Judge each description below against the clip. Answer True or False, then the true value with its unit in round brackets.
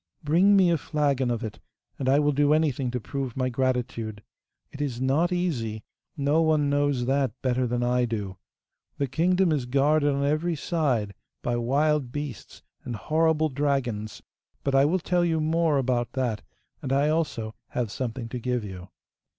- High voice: False (135 Hz)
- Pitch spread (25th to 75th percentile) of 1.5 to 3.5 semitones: False (3.9 semitones)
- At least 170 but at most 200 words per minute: True (175 wpm)